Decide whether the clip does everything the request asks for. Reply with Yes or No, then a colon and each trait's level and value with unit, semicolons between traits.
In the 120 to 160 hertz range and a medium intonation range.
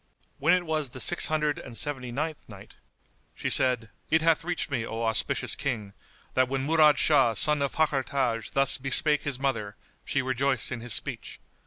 Yes: low, 135 Hz; average, 3.7 semitones